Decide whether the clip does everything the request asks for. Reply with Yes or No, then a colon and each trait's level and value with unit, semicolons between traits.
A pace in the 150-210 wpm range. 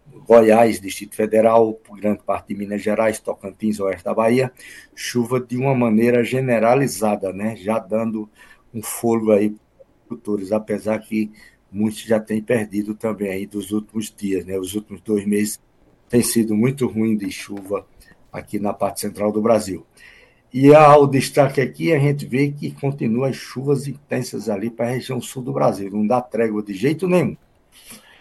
Yes: average, 170 wpm